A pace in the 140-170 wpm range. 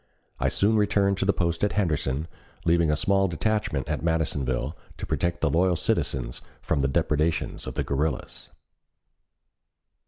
Yes: average, 150 wpm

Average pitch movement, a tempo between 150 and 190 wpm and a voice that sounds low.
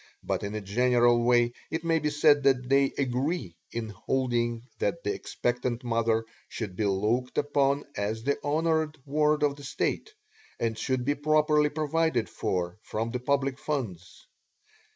Yes: average, 4.3 semitones; average, 155 wpm; low, 130 Hz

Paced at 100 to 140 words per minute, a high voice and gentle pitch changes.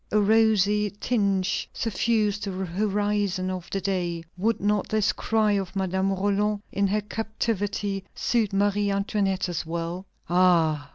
Yes: slow, 135 wpm; high, 200 Hz; narrow, 2.0 semitones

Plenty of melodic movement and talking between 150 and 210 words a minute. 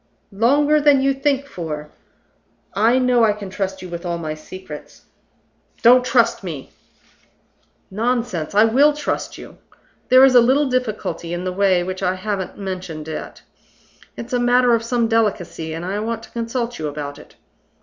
Yes: wide, 5.8 semitones; average, 170 wpm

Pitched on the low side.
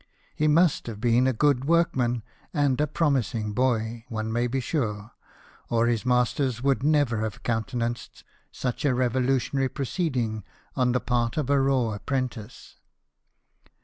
Yes: low, 125 Hz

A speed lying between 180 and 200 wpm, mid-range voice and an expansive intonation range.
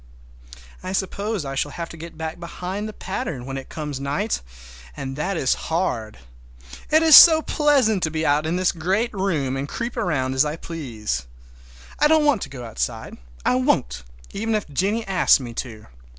Yes: average, 185 wpm; medium, 165 Hz; wide, 7.1 semitones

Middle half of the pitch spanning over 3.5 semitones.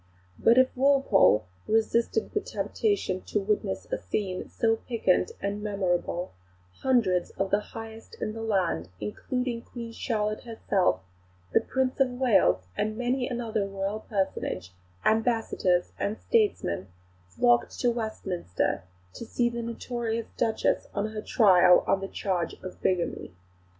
Yes: average, 4.2 semitones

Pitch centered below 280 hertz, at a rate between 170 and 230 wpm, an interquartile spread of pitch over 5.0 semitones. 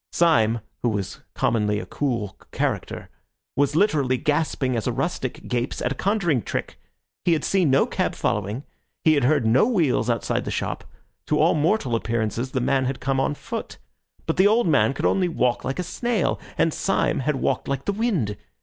Yes: low, 135 Hz; average, 190 wpm; wide, 5.6 semitones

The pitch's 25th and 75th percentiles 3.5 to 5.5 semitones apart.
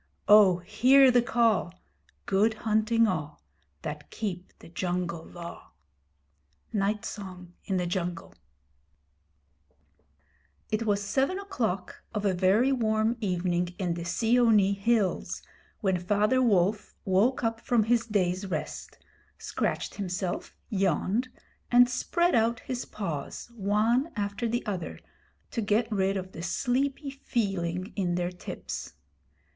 Yes: average, 4.2 semitones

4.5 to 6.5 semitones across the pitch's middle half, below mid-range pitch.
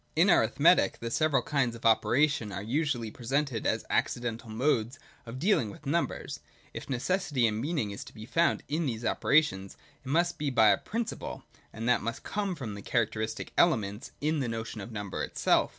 Yes: average, 5.2 semitones; low, 120 Hz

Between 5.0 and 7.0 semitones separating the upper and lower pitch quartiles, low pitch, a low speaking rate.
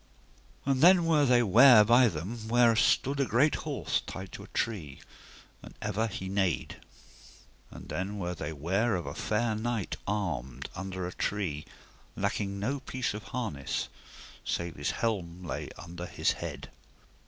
No: average, 5.3 semitones; low, 105 Hz; average, 155 wpm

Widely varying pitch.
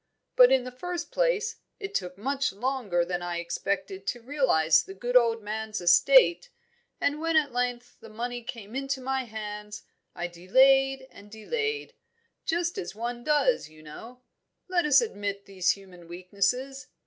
Yes: wide, 5.7 semitones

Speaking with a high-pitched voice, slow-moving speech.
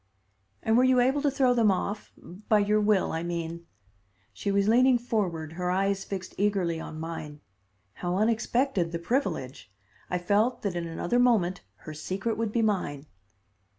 No: high, 200 Hz; average, 165 wpm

